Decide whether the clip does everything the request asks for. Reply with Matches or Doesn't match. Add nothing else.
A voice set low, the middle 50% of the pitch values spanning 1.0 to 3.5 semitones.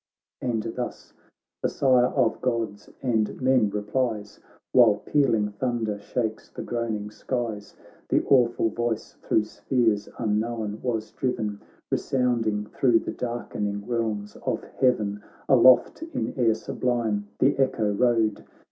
Matches